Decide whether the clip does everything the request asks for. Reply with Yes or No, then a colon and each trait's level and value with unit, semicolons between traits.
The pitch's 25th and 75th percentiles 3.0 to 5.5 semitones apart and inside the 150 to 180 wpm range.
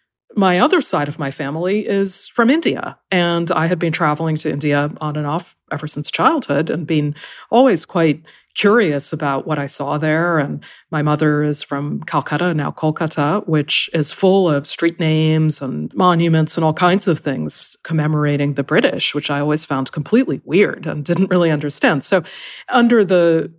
Yes: average, 3.3 semitones; average, 175 wpm